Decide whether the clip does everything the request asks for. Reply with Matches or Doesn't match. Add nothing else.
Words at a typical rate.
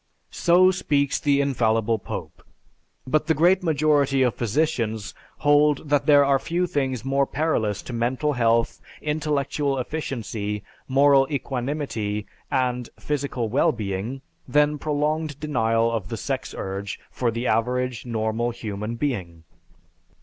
Doesn't match